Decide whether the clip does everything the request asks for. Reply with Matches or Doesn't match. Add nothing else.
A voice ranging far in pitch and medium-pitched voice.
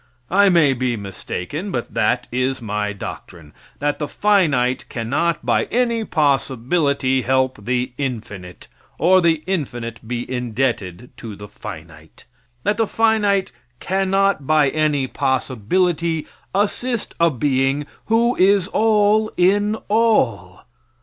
Matches